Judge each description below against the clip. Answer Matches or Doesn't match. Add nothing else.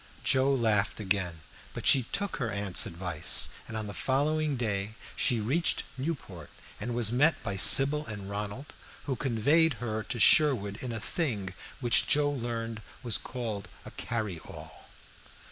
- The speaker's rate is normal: Matches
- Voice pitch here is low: Matches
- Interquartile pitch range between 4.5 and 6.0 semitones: Matches